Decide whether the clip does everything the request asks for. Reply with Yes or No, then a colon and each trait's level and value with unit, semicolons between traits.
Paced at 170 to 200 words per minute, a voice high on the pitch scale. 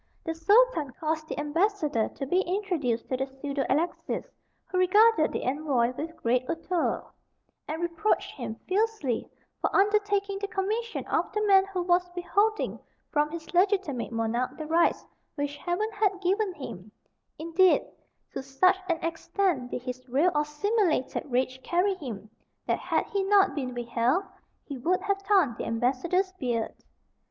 No: average, 155 wpm; very high, 330 Hz